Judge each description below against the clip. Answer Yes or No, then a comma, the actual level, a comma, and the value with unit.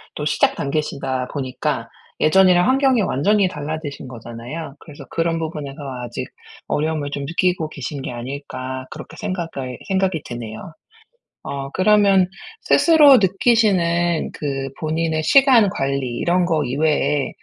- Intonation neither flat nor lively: Yes, average, 5.0 semitones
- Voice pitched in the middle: Yes, medium, 155 Hz